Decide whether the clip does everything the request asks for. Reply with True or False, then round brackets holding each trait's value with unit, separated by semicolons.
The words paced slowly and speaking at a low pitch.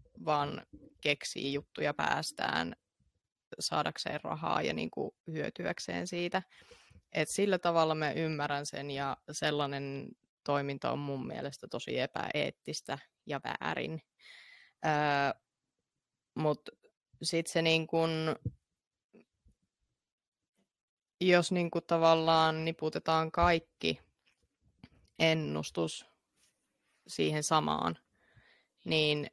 False (80 wpm; 150 Hz)